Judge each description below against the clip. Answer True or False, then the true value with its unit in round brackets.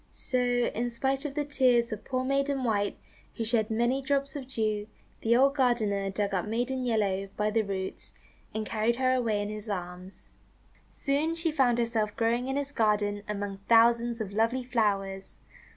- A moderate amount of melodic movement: True (3.6 semitones)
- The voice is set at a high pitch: True (230 Hz)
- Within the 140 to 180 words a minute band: True (175 wpm)